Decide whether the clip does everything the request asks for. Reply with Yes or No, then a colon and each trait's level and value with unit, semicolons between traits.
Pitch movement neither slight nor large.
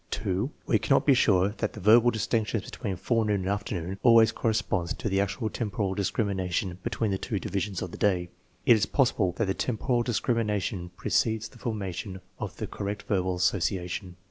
Yes: average, 3.1 semitones